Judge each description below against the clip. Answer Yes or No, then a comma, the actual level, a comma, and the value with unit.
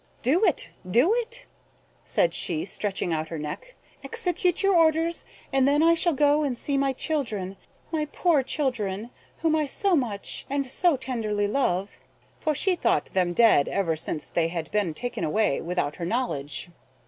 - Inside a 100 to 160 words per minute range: No, average, 170 wpm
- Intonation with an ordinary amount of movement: No, wide, 9.0 semitones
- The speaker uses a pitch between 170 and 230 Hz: No, very high, 260 Hz